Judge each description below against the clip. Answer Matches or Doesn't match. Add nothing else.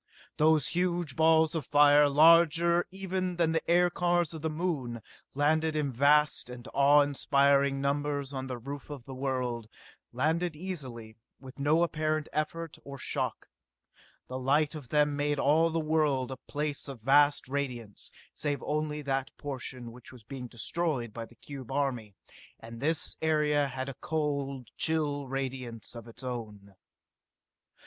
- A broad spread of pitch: Doesn't match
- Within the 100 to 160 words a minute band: Matches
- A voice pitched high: Doesn't match